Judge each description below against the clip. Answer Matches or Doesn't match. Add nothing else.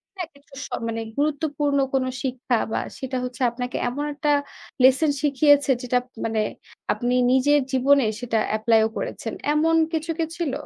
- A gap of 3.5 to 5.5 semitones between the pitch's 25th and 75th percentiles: Doesn't match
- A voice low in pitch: Doesn't match